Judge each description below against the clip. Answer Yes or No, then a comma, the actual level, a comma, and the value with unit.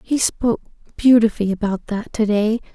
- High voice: Yes, high, 220 Hz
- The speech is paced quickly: No, slow, 130 wpm